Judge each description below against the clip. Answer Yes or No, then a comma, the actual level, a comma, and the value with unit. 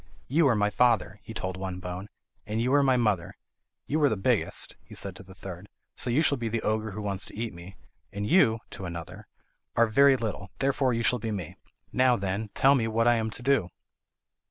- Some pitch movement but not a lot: Yes, average, 4.3 semitones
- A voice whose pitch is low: Yes, low, 110 Hz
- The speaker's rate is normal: No, fast, 225 wpm